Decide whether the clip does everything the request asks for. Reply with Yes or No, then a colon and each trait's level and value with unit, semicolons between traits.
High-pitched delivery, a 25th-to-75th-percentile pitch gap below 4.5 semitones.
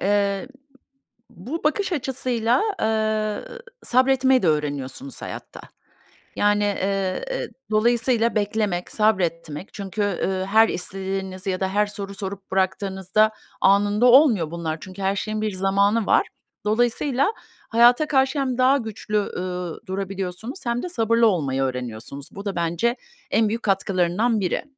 Yes: high, 205 Hz; average, 3.8 semitones